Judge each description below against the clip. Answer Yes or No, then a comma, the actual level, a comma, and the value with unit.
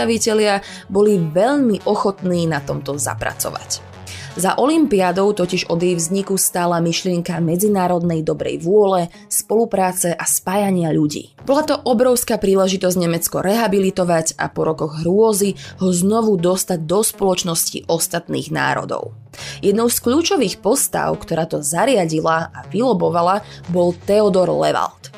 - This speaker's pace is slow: No, average, 120 wpm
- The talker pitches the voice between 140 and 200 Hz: Yes, medium, 185 Hz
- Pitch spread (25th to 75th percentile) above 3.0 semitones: Yes, average, 3.5 semitones